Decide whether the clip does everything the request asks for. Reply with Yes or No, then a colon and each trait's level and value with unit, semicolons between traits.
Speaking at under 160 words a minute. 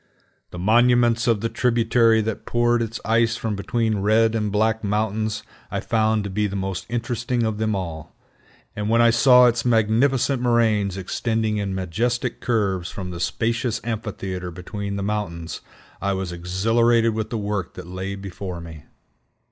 No: average, 165 wpm